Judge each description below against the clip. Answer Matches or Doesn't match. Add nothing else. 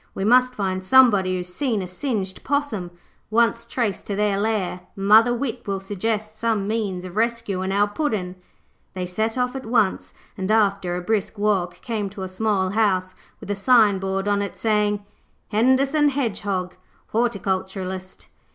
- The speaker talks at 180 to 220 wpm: Doesn't match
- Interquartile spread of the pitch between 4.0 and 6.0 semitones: Doesn't match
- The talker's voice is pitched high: Matches